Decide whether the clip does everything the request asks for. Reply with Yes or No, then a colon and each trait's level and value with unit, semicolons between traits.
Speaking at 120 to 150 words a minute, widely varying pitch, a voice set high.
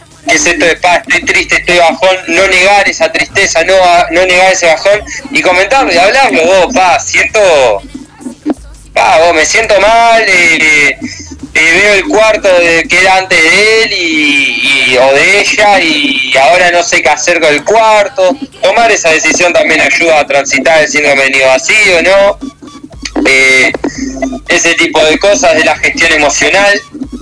No: average, 170 wpm; wide, 8.1 semitones; high, 195 Hz